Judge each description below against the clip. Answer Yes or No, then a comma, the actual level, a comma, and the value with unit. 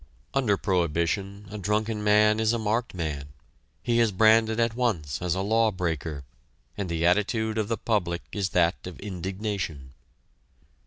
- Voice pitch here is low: Yes, low, 100 Hz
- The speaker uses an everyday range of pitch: Yes, average, 4.2 semitones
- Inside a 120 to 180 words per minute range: Yes, average, 155 wpm